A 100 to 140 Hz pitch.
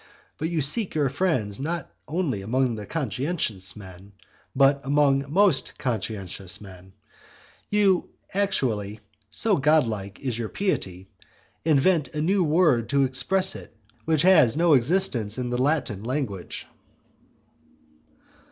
Yes: low, 135 Hz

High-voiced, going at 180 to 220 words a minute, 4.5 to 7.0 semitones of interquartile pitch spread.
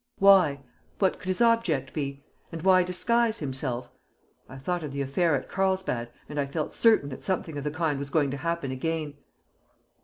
No: medium, 155 Hz; average, 185 wpm; average, 4.9 semitones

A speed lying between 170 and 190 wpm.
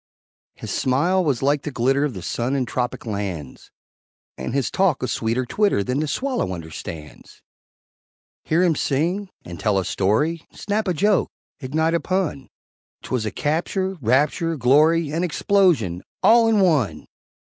No: average, 155 wpm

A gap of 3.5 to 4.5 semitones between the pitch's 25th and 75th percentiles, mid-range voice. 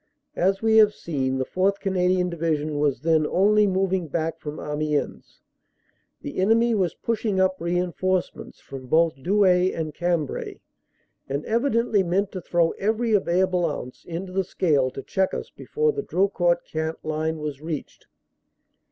Yes: average, 3.8 semitones; medium, 175 Hz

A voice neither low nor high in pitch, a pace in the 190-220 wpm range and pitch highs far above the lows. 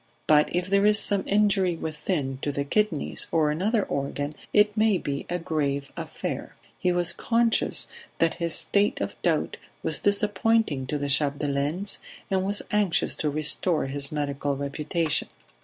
No: medium, 165 Hz; average, 155 wpm; wide, 5.8 semitones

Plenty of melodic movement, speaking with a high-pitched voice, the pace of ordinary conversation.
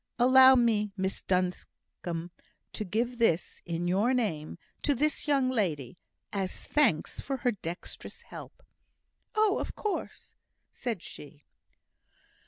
No: wide, 6.6 semitones; high, 215 Hz; slow, 120 wpm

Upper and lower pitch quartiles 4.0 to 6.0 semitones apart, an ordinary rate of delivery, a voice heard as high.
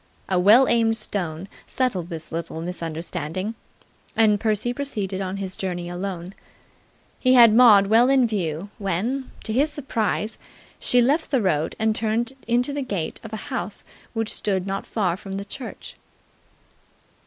Yes: average, 4.5 semitones; average, 155 wpm; high, 205 Hz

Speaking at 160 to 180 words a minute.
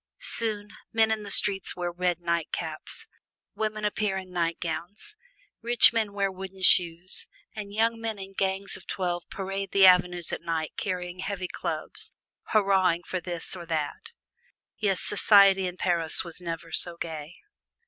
No: average, 150 wpm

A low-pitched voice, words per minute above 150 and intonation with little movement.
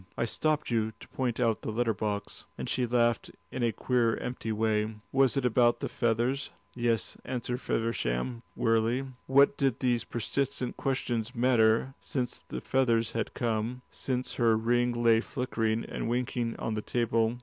Yes: low, 120 Hz; average, 160 wpm; narrow, 1.9 semitones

